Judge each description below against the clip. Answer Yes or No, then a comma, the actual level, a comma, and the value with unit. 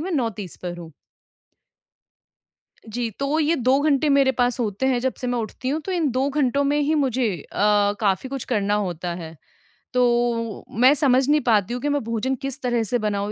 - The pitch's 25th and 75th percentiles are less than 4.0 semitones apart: No, average, 4.3 semitones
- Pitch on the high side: Yes, very high, 255 Hz